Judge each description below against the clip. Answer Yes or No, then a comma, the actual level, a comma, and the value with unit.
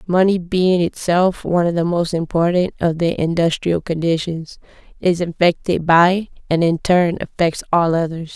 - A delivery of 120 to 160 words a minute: Yes, average, 150 wpm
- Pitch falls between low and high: Yes, medium, 170 Hz